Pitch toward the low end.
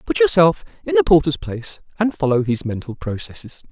No: medium, 160 Hz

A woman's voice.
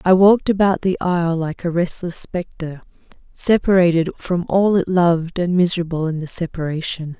Yes: female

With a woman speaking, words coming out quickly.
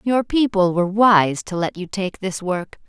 Yes: female; fast, 210 wpm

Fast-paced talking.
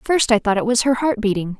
Yes: fast, 300 wpm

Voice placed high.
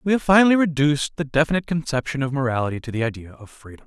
No: medium, 145 Hz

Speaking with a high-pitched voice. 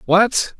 Yes: high, 200 Hz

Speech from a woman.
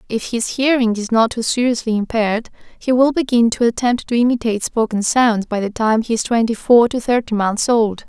Yes: female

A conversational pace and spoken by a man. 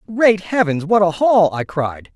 Yes: average, 195 wpm; male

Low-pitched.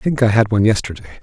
Yes: low, 105 Hz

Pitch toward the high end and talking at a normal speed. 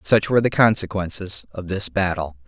No: very low, 95 Hz; average, 170 wpm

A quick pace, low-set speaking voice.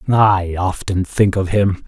No: average, 160 wpm; very low, 95 Hz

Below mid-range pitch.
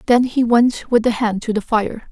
No: high, 230 Hz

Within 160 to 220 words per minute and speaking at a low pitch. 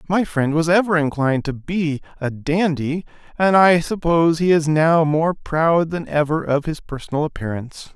No: average, 175 wpm; medium, 160 Hz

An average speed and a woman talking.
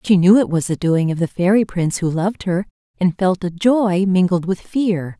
No: fast, 230 wpm; female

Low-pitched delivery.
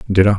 Yes: low, 100 Hz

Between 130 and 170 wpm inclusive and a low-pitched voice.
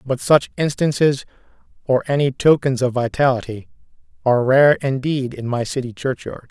Yes: average, 140 wpm; low, 130 Hz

